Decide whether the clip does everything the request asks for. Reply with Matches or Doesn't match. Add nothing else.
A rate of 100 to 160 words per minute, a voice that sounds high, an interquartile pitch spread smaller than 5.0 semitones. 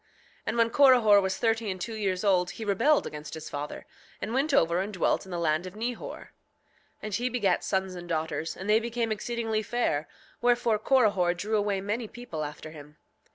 Doesn't match